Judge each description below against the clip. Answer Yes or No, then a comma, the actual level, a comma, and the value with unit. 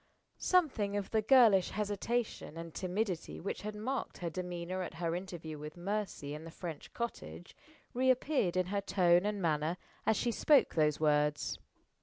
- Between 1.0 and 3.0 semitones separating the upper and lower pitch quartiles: No, average, 4.4 semitones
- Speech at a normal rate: Yes, average, 165 wpm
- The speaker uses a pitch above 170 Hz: Yes, medium, 185 Hz